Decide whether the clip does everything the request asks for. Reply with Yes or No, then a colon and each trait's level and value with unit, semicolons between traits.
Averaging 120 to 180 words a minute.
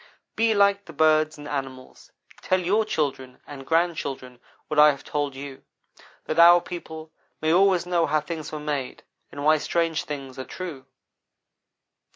Yes: average, 160 wpm